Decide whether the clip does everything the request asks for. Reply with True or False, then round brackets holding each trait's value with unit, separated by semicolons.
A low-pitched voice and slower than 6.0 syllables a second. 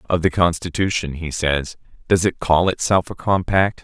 True (85 Hz; 4.7 syllables/s)